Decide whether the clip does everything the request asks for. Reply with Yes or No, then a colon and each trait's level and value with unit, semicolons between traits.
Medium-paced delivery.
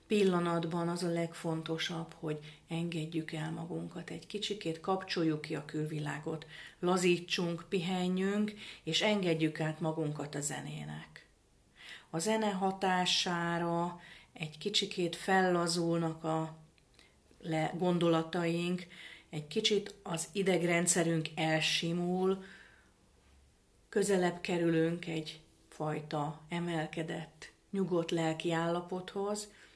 No: slow, 85 wpm